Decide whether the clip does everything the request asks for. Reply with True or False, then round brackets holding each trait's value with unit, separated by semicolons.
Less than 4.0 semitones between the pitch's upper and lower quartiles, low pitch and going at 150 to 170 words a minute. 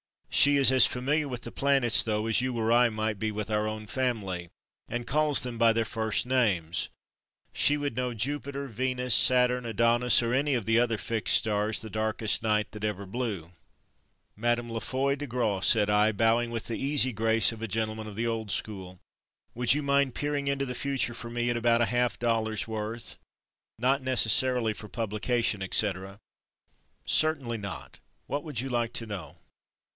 False (2.8 semitones; 115 Hz; 180 wpm)